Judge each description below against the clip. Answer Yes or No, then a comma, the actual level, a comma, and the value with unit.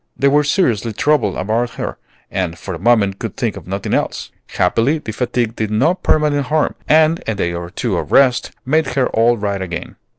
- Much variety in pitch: Yes, wide, 6.4 semitones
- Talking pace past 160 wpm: Yes, average, 200 wpm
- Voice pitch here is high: No, low, 120 Hz